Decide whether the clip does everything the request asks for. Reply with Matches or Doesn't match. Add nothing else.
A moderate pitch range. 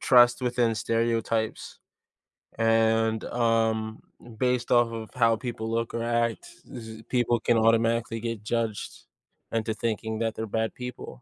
Doesn't match